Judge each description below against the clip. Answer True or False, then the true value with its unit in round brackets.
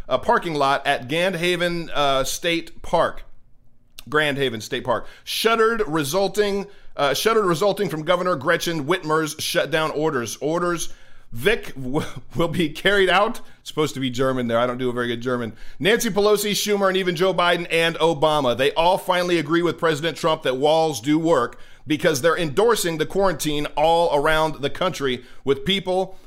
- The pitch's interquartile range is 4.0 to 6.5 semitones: True (4.7 semitones)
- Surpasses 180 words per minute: False (170 wpm)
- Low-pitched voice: False (165 Hz)